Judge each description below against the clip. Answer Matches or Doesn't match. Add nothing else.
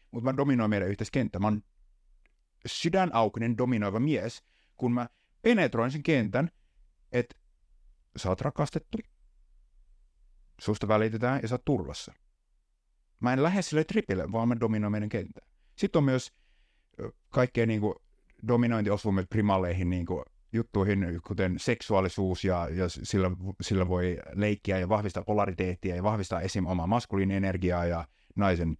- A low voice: Matches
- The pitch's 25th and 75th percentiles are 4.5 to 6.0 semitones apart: Matches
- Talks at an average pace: Matches